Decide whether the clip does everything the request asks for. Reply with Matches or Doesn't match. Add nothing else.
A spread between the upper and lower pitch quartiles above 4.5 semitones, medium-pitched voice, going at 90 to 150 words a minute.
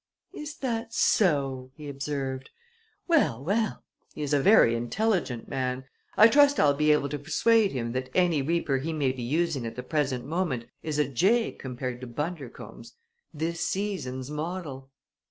Doesn't match